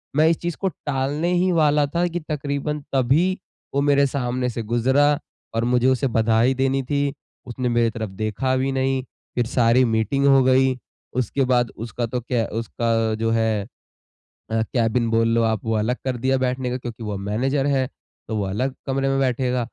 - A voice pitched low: Yes, low, 130 Hz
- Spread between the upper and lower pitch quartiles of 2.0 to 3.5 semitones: Yes, average, 3.0 semitones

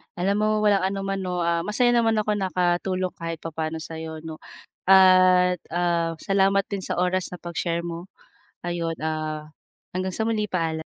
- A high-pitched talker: No, medium, 180 Hz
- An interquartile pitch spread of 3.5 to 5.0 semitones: No, average, 2.7 semitones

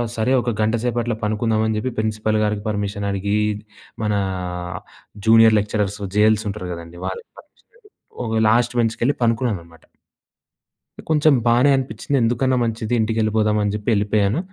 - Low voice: Yes, low, 110 Hz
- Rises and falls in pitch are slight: Yes, narrow, 2.1 semitones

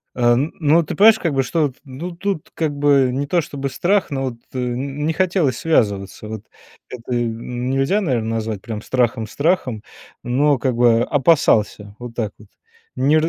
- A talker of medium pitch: No, low, 130 Hz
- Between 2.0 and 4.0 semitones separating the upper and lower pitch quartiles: No, average, 4.6 semitones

